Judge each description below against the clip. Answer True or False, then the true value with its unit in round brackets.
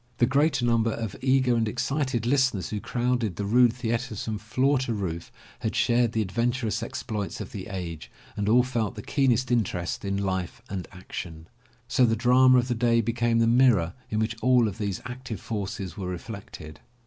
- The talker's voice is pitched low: True (115 Hz)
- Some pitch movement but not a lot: True (3.6 semitones)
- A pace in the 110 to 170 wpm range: False (185 wpm)